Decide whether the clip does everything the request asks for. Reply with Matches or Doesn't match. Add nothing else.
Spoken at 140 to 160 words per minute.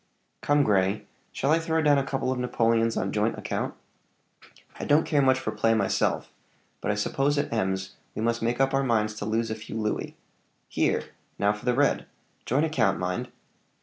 Doesn't match